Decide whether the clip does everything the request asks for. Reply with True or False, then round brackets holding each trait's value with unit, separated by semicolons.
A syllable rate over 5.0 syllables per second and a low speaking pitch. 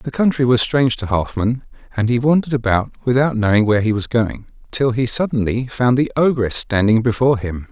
True (5.7 syllables/s; 120 Hz)